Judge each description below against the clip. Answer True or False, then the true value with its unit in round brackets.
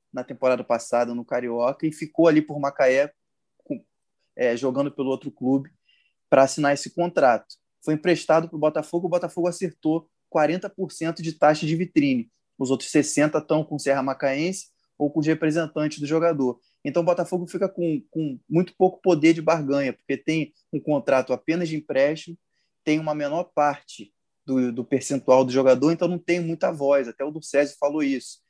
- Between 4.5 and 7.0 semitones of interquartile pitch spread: False (3.4 semitones)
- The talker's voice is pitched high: False (155 Hz)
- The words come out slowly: False (180 wpm)